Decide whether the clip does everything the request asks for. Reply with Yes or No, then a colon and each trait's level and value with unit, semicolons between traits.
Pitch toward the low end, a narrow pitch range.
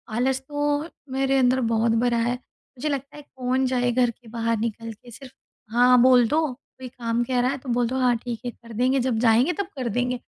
No: very high, 250 Hz; narrow, 1.8 semitones